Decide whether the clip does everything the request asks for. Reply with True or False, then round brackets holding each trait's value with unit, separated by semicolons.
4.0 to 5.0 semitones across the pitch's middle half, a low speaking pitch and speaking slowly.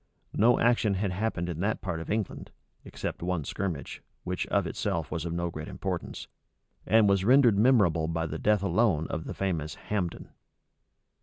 False (4.3 semitones; 90 Hz; 170 wpm)